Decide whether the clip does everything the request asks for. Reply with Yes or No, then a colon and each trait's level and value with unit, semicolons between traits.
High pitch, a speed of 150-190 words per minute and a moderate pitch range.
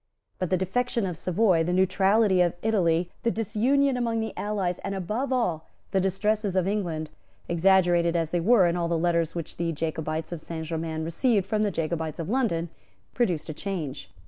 No: medium, 180 Hz; average, 185 wpm; average, 4.2 semitones